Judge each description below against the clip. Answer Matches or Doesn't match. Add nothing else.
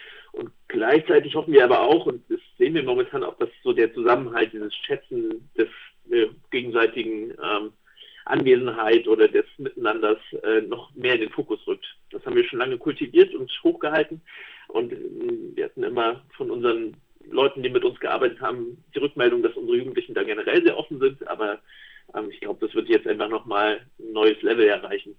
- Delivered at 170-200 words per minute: Matches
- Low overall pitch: Doesn't match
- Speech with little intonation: Matches